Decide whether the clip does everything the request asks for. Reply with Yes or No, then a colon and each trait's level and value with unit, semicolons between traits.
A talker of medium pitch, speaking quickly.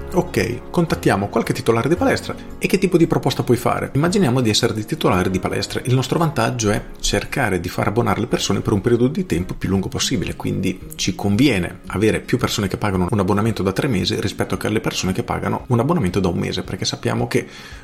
No: low, 110 Hz; fast, 220 wpm